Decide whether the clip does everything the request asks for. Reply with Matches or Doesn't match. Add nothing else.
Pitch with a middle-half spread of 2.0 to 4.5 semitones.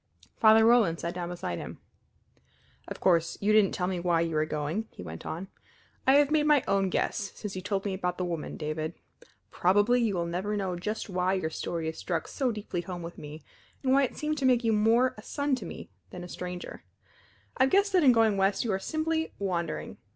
Doesn't match